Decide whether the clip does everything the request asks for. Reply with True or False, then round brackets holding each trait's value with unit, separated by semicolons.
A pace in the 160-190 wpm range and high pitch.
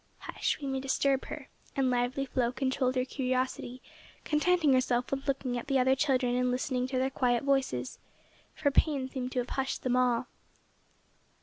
True (175 wpm; 260 Hz)